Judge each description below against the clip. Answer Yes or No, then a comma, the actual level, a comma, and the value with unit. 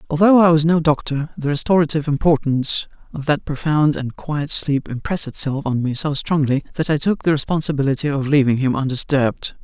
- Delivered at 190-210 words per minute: No, average, 180 wpm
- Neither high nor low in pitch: Yes, medium, 145 Hz